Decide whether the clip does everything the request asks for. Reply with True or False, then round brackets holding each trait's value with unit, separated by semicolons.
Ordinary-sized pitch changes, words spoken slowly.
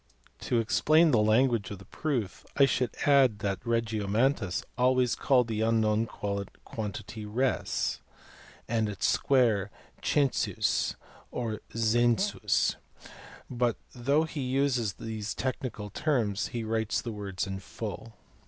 True (3.4 semitones; 120 wpm)